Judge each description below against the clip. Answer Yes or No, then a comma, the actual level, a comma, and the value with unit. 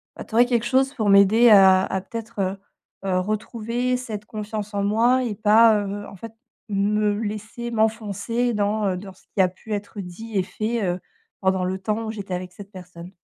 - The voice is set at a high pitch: Yes, high, 210 Hz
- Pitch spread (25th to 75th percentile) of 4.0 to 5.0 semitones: No, average, 2.7 semitones